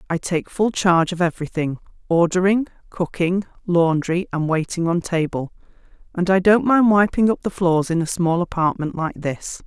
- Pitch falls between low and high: Yes, medium, 175 Hz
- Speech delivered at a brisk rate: No, average, 160 wpm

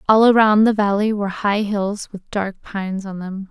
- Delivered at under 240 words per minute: Yes, fast, 205 wpm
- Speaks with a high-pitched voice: Yes, high, 205 Hz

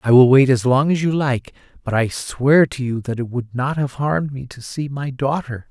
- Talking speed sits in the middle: No, fast, 250 wpm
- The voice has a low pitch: Yes, low, 130 Hz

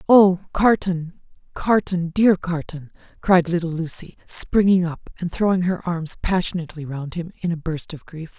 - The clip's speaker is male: No, female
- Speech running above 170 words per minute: No, average, 155 wpm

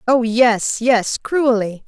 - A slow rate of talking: Yes, slow, 130 wpm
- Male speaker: No, female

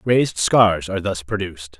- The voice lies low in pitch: Yes, low, 100 Hz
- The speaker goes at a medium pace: Yes, average, 165 wpm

